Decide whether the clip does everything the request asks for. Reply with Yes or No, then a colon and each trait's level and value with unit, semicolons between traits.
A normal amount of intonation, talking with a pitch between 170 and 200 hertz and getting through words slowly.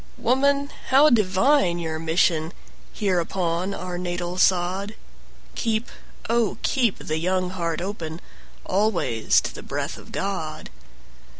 Yes: average, 4.3 semitones; medium, 185 Hz; slow, 120 wpm